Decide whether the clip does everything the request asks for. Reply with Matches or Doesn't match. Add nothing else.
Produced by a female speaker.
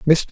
Doesn't match